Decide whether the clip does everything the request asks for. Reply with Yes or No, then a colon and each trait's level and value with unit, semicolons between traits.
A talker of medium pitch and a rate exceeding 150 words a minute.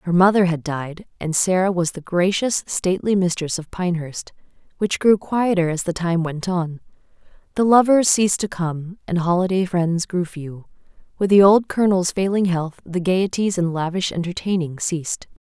Yes: medium, 180 Hz; average, 165 wpm